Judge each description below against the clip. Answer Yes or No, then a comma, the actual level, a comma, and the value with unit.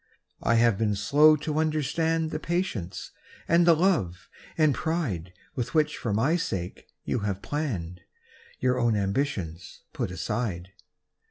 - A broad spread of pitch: Yes, wide, 8.1 semitones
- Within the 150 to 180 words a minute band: No, slow, 135 wpm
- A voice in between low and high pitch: No, low, 125 Hz